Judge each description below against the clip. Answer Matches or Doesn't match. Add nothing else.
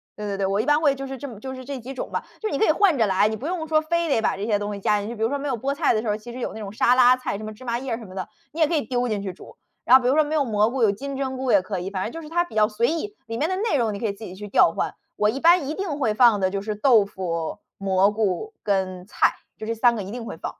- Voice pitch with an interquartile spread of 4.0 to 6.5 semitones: Matches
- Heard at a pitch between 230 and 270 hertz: Matches